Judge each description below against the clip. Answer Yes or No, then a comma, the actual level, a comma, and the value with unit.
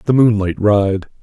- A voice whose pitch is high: No, low, 105 Hz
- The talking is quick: No, average, 145 wpm